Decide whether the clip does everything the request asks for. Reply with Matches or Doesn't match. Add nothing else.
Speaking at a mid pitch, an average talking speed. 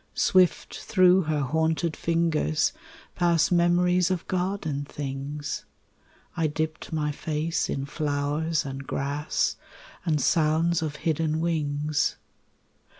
Doesn't match